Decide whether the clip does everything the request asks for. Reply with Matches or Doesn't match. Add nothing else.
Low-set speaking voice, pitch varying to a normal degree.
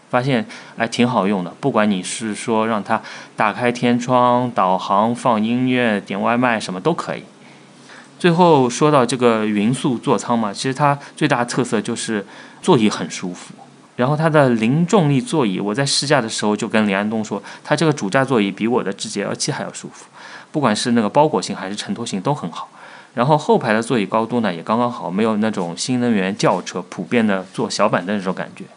Matches